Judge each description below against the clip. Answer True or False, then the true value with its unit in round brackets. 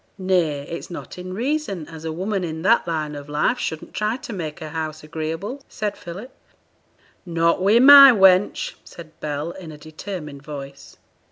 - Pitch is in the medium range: True (170 Hz)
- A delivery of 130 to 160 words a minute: False (170 wpm)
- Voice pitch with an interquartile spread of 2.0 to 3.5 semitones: False (4.4 semitones)